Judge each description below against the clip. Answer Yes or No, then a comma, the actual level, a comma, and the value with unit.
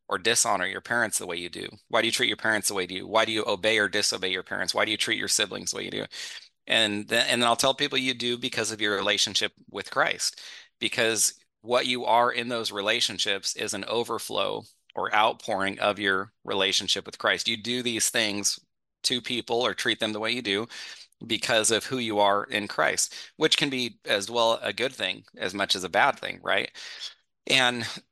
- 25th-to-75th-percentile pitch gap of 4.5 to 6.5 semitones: No, average, 2.9 semitones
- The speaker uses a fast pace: Yes, fast, 220 wpm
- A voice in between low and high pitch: No, low, 115 Hz